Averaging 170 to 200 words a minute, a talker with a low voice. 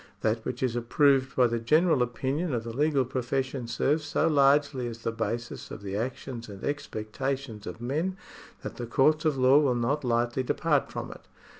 Yes: average, 185 wpm; low, 130 Hz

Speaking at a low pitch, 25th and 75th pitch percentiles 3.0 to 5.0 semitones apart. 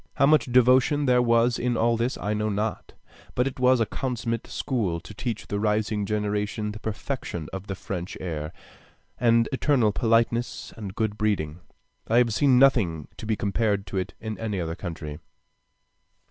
Yes: low, 110 Hz; average, 3.3 semitones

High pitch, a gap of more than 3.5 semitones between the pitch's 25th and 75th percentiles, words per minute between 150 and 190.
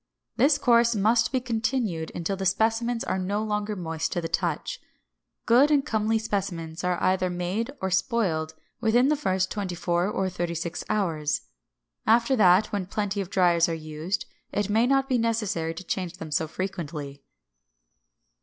Yes: high, 195 Hz; average, 4.7 semitones; average, 165 wpm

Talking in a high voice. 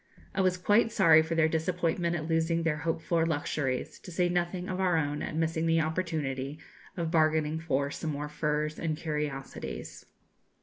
No: medium, 160 Hz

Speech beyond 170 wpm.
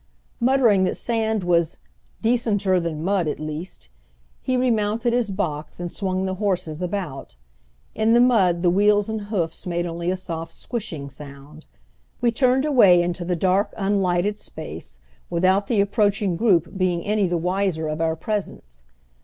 No: average, 155 wpm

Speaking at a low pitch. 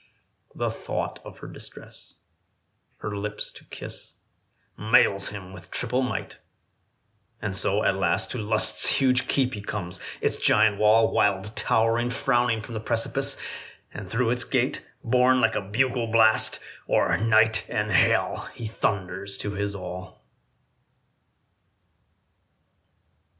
Yes: low, 110 Hz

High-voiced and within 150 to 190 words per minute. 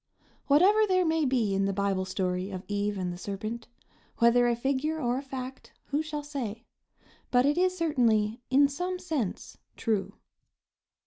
Yes: high, 245 Hz; average, 165 wpm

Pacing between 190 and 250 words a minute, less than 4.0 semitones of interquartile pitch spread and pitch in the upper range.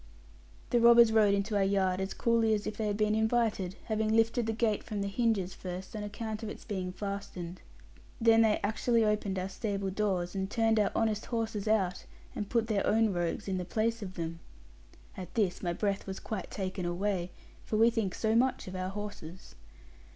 Yes: average, 200 wpm; average, 2.8 semitones; high, 210 Hz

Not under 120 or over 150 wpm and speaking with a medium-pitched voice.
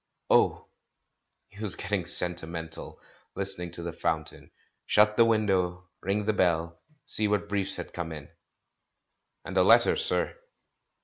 No: slow, 135 wpm; very low, 95 Hz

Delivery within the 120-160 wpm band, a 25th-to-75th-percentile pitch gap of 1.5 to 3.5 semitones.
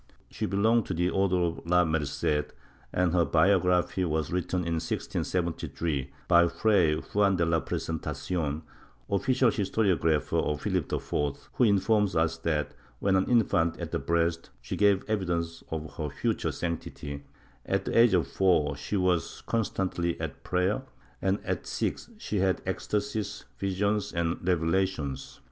Yes: average, 145 wpm; average, 3.2 semitones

